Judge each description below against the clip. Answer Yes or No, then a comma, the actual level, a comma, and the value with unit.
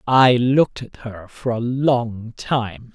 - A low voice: Yes, low, 120 Hz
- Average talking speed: Yes, average, 165 wpm